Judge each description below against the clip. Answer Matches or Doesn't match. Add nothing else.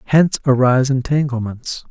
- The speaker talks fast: Doesn't match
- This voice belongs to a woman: Doesn't match